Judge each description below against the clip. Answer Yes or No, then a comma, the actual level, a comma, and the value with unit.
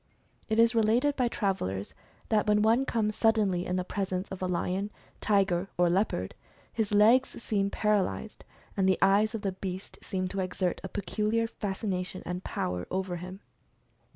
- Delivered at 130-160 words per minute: No, average, 180 wpm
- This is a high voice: Yes, high, 195 Hz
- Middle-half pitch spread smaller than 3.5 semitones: Yes, average, 2.8 semitones